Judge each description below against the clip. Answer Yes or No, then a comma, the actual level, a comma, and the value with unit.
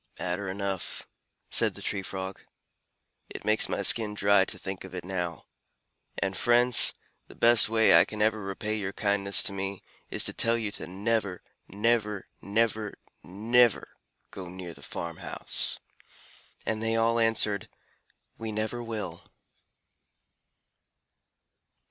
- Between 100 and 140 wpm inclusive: Yes, slow, 135 wpm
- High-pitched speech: No, low, 100 Hz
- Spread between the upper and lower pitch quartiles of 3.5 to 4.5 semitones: No, average, 2.9 semitones